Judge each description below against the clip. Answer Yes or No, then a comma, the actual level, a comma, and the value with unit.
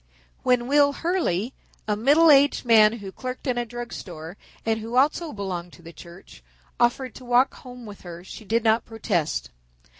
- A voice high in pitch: Yes, high, 230 Hz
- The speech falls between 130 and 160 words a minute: No, average, 180 wpm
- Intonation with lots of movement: No, average, 4.8 semitones